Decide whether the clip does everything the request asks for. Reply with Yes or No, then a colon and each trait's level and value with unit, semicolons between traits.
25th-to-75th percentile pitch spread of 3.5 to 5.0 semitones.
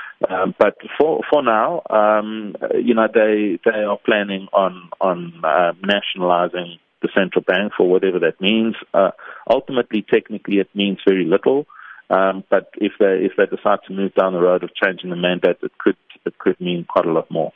No: average, 2.7 semitones